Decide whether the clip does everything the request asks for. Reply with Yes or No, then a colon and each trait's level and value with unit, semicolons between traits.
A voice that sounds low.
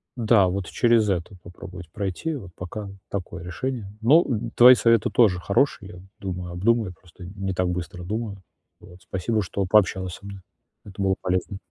Yes: very low, 95 Hz